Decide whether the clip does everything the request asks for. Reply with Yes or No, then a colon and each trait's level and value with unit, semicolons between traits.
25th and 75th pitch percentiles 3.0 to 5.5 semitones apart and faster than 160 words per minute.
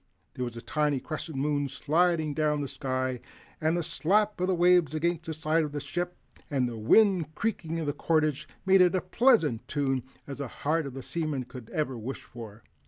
Yes: average, 4.2 semitones; average, 195 wpm